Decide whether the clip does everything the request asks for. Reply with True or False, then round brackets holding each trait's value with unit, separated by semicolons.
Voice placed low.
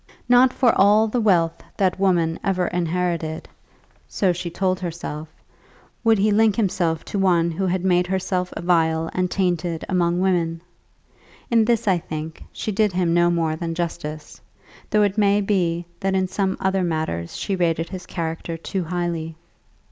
False (180 Hz)